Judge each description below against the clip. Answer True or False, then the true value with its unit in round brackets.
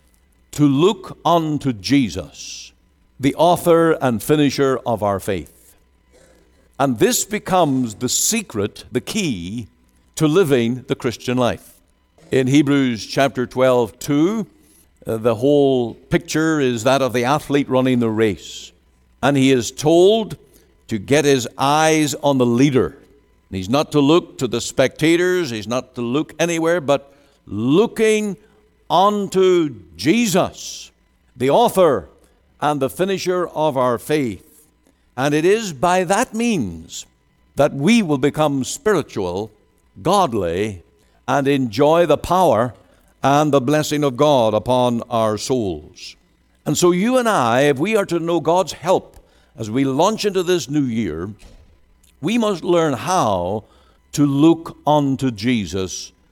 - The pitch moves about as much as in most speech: False (5.9 semitones)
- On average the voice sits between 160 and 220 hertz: False (140 Hz)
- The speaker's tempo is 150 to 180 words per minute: False (135 wpm)